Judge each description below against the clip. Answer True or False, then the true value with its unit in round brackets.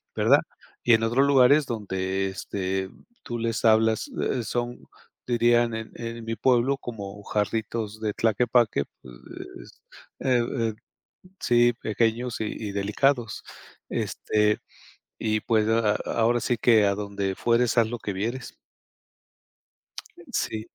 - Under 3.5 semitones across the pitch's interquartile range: True (2.5 semitones)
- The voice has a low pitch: True (115 Hz)